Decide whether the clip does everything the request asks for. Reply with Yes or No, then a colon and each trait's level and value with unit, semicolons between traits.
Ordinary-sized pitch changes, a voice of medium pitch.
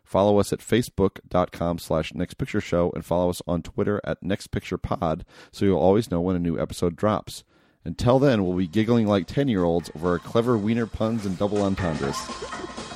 No: average, 3.4 semitones; very low, 95 Hz